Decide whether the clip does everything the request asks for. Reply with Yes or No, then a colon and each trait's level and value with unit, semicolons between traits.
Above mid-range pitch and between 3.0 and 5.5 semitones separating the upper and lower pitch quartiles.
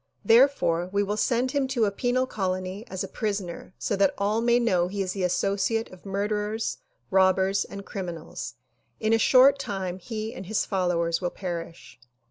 Yes: high, 200 Hz; average, 3.4 semitones